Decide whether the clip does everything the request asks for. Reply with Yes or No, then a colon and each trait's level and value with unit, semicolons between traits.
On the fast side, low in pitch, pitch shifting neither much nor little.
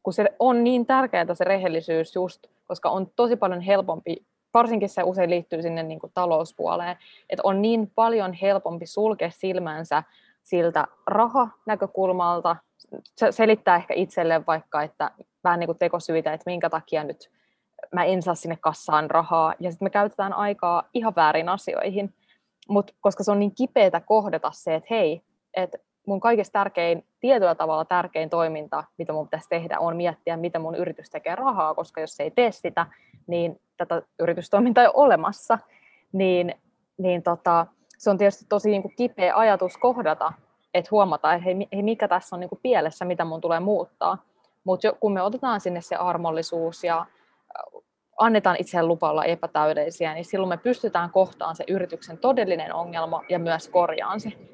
No: fast, 165 wpm; medium, 180 Hz; average, 3.6 semitones